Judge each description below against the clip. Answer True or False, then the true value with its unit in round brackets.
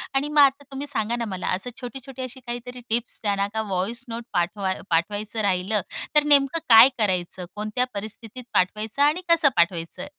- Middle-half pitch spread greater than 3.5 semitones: True (4.7 semitones)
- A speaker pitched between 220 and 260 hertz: True (225 Hz)